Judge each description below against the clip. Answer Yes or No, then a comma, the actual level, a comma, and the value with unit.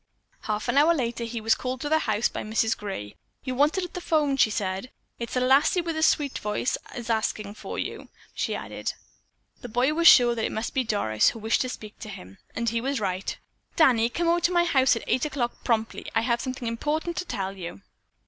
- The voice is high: Yes, high, 240 Hz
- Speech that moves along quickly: Yes, fast, 235 wpm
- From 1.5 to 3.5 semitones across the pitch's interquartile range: No, average, 4.8 semitones